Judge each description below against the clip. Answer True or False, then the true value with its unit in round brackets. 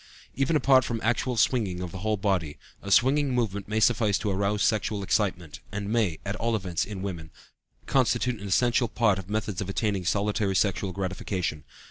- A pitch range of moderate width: True (3.2 semitones)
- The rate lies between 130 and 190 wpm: True (180 wpm)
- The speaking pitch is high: False (105 Hz)